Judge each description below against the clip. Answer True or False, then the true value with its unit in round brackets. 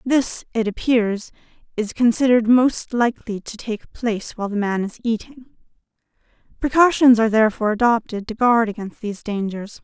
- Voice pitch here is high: True (225 Hz)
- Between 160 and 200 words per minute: False (145 wpm)